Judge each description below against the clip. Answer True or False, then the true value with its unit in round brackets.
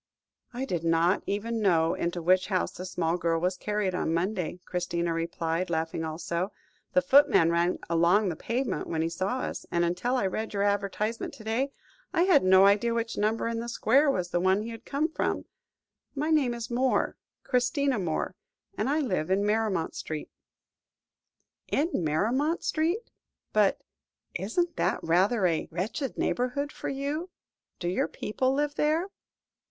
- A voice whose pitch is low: False (205 Hz)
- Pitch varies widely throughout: True (6.7 semitones)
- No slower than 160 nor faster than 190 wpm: True (165 wpm)